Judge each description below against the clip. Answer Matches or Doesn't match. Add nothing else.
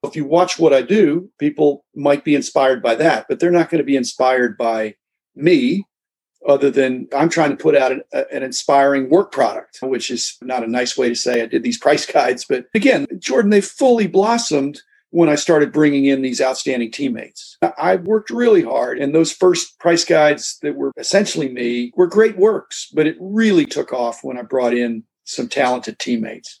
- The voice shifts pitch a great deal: Matches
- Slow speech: Doesn't match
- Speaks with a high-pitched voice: Doesn't match